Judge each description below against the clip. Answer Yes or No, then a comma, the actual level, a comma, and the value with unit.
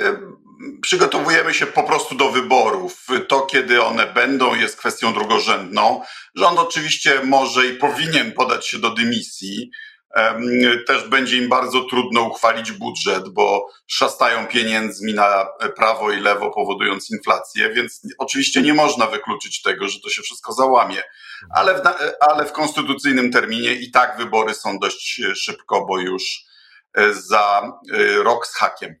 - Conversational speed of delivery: Yes, average, 140 wpm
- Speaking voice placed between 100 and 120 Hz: No, low, 135 Hz